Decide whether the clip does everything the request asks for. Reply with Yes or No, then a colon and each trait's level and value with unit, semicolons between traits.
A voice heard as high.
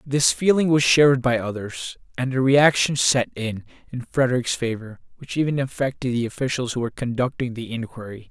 No: low, 125 Hz